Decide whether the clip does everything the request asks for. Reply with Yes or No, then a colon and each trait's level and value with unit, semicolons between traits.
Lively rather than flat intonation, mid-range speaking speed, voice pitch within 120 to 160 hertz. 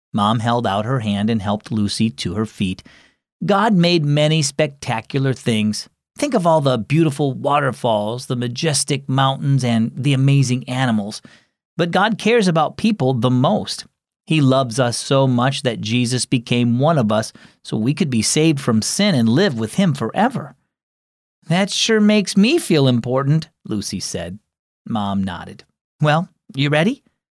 Yes: wide, 5.8 semitones; average, 160 wpm; low, 135 Hz